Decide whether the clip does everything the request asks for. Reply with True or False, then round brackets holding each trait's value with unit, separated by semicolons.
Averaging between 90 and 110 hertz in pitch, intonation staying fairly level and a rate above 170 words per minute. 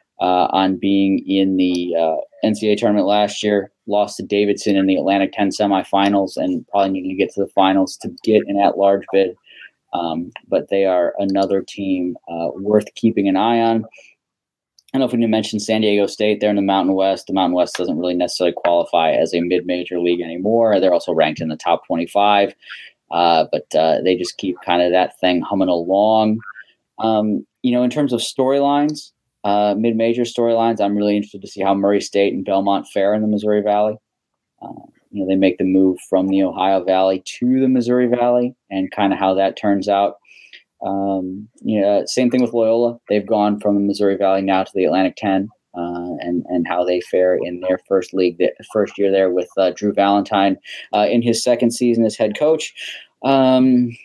True (100 Hz; 2.3 semitones; 200 wpm)